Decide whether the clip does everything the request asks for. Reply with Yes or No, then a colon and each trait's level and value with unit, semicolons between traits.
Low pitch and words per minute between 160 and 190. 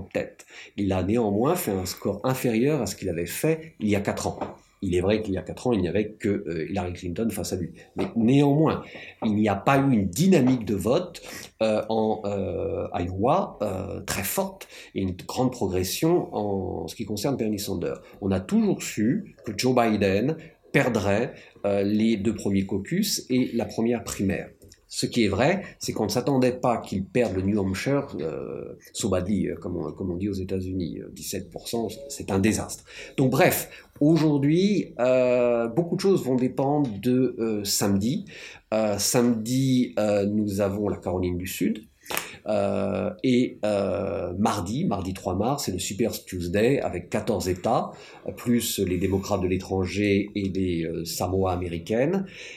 Yes: low, 105 Hz; average, 175 wpm